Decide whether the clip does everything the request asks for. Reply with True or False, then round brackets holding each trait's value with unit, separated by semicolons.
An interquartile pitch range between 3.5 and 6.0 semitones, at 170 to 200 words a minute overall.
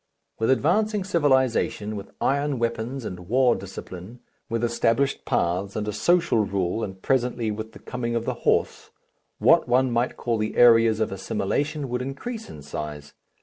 False (4.2 semitones; 160 wpm)